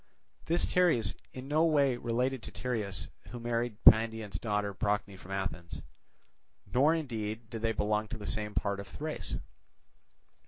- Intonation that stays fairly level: No, average, 3.6 semitones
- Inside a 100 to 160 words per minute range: Yes, average, 155 wpm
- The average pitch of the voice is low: Yes, low, 115 Hz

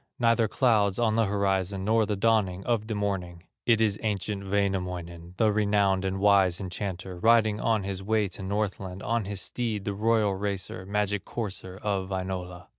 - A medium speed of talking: Yes, average, 170 wpm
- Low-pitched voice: Yes, low, 100 Hz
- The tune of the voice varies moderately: No, narrow, 2.3 semitones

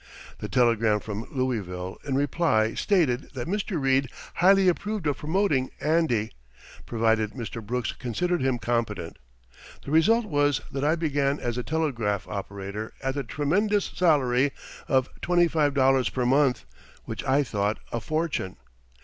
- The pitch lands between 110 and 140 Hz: Yes, low, 135 Hz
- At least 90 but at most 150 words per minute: Yes, average, 145 wpm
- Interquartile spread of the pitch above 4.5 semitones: Yes, wide, 5.4 semitones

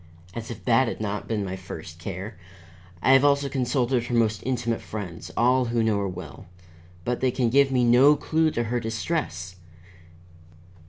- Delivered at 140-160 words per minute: No, average, 175 wpm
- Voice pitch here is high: No, low, 120 Hz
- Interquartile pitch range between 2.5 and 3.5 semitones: No, average, 3.9 semitones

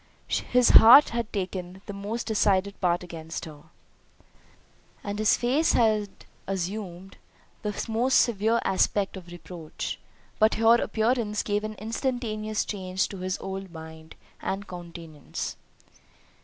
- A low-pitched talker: No, high, 200 Hz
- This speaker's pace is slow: Yes, slow, 125 wpm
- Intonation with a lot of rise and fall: No, average, 3.5 semitones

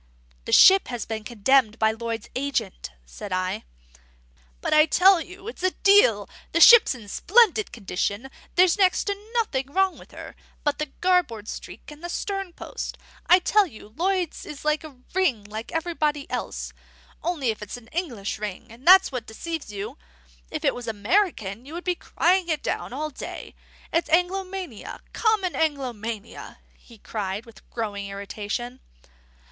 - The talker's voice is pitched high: Yes, very high, 285 Hz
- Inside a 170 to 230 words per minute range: No, average, 155 wpm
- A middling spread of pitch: No, wide, 8.5 semitones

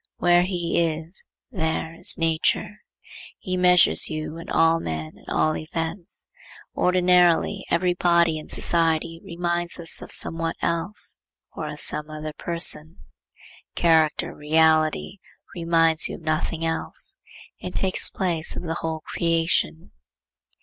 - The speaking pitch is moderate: Yes, medium, 165 Hz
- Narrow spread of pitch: Yes, narrow, 1.6 semitones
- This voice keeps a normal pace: No, slow, 130 wpm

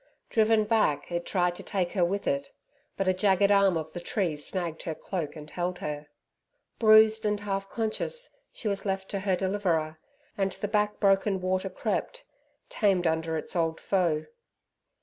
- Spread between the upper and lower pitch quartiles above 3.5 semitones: No, average, 3.2 semitones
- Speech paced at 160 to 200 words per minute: Yes, average, 170 wpm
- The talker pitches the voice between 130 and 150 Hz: No, high, 190 Hz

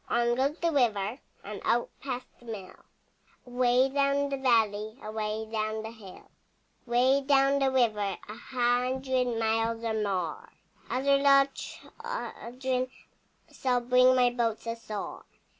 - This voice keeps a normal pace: No, slow, 130 wpm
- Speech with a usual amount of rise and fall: Yes, average, 3.1 semitones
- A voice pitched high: Yes, high, 245 Hz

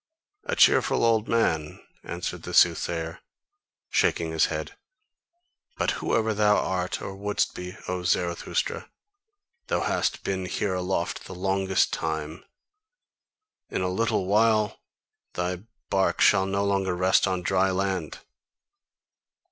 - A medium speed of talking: No, slow, 125 wpm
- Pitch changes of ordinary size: No, narrow, 1.9 semitones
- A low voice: Yes, very low, 95 Hz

